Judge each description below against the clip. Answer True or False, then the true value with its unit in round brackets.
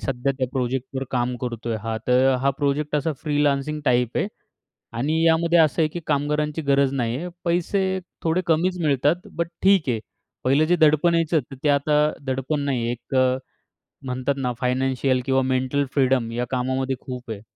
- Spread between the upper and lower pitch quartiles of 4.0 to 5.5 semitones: False (3.2 semitones)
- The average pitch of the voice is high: False (135 Hz)